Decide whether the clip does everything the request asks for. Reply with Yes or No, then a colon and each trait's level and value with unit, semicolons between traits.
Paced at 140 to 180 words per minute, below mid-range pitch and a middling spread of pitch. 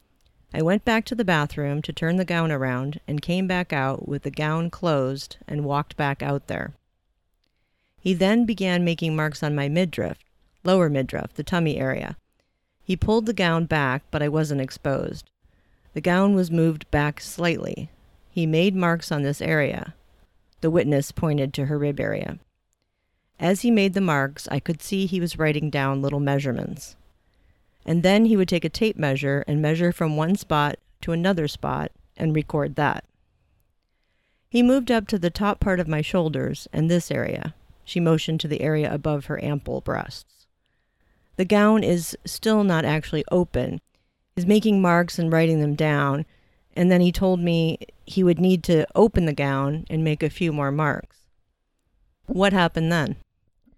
No: average, 175 wpm; medium, 160 Hz; average, 3.9 semitones